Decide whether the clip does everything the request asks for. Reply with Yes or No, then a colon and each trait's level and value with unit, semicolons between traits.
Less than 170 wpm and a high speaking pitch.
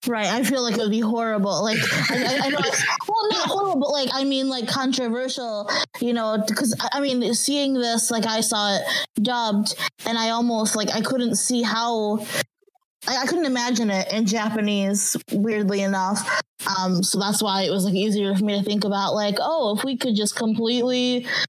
No: average, 200 wpm; high, 225 Hz